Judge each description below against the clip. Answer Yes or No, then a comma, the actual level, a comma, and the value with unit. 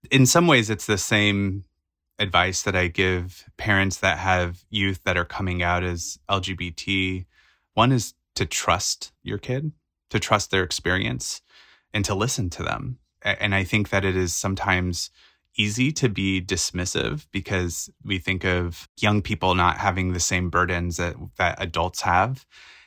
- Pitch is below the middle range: Yes, very low, 95 Hz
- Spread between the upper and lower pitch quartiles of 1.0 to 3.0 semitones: Yes, average, 2.7 semitones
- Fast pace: No, average, 160 wpm